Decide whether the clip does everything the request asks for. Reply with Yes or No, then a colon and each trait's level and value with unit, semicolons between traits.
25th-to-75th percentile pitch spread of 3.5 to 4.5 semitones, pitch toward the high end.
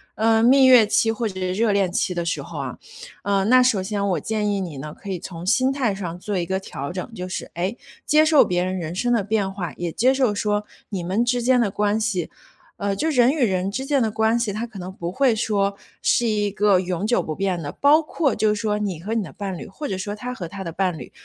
Yes: average, 3.9 semitones; high, 205 Hz